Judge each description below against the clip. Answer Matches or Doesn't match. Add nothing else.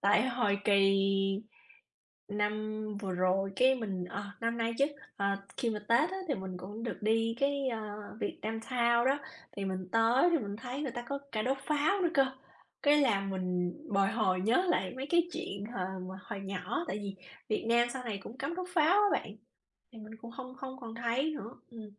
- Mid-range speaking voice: Doesn't match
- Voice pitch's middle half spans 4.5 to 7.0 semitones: Matches